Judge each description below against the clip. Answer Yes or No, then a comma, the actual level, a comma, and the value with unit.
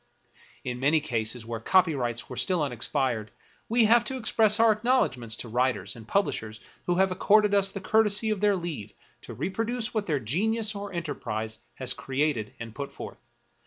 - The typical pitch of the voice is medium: Yes, medium, 160 Hz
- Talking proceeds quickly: No, average, 175 wpm